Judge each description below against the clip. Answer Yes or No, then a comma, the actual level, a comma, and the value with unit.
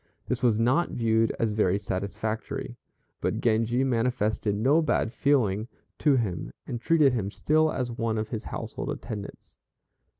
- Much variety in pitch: No, average, 3.0 semitones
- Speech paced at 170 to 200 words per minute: No, average, 145 wpm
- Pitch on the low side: Yes, low, 115 Hz